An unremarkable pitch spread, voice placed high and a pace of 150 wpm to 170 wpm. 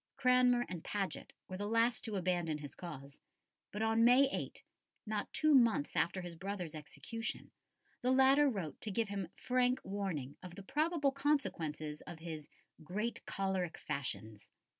No: wide, 6.8 semitones; high, 200 Hz; average, 155 wpm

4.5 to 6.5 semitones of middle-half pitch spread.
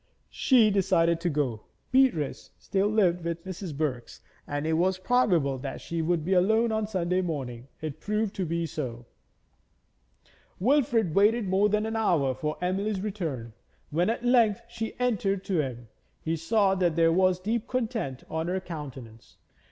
Yes: average, 5.3 semitones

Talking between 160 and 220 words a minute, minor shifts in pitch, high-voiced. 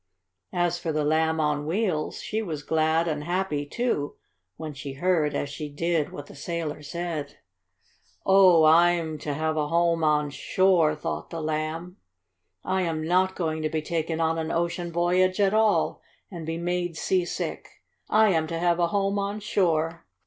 No: average, 170 wpm; narrow, 2.3 semitones; medium, 165 Hz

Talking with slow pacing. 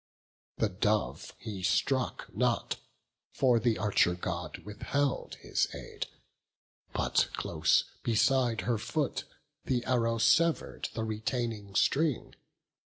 Yes: slow, 105 wpm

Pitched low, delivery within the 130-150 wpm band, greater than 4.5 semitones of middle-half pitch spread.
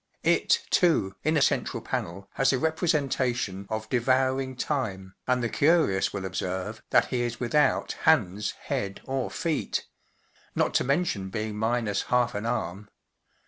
Yes: low, 120 Hz; average, 140 wpm; average, 5.2 semitones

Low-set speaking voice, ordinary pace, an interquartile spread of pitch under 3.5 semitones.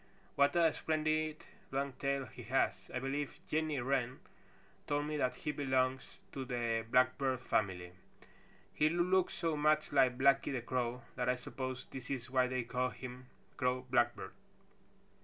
Yes: low, 130 Hz; average, 155 wpm; narrow, 2.5 semitones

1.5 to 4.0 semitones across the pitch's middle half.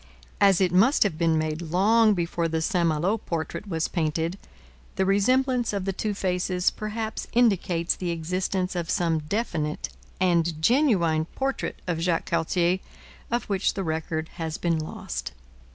Yes: average, 3.6 semitones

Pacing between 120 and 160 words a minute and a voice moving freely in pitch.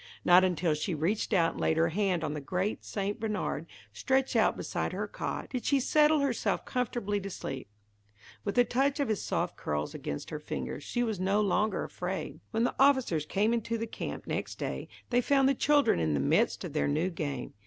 No: fast, 205 wpm; wide, 6.9 semitones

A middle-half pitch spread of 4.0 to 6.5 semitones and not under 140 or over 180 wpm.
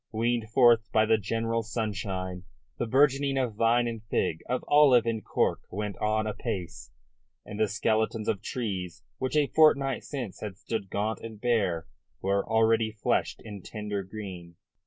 No: average, 2.7 semitones; average, 155 wpm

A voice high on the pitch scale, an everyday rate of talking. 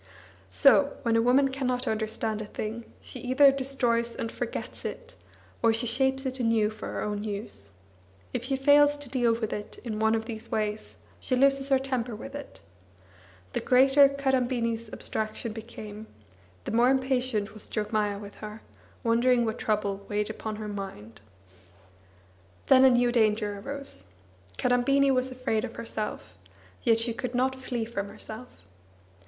Yes: high, 235 Hz; average, 160 wpm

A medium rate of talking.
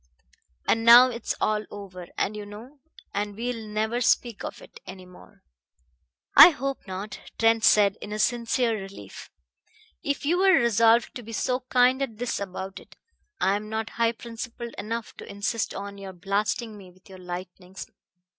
Yes: average, 165 wpm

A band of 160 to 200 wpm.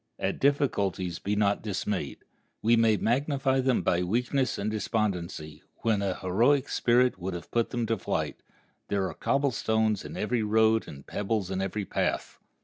Yes: average, 165 wpm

